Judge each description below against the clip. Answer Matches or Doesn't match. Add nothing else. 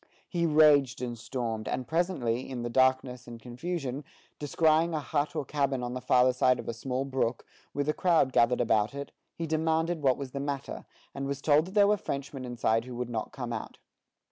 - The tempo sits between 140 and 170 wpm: Doesn't match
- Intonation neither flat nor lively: Matches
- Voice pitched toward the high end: Doesn't match